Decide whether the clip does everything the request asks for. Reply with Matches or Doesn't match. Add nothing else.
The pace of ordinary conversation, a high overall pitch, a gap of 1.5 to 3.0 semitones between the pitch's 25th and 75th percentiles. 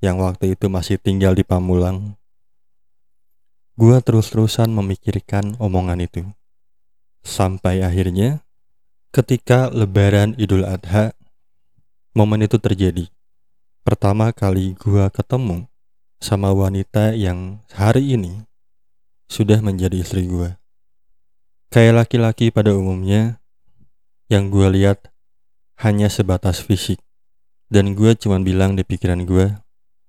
Doesn't match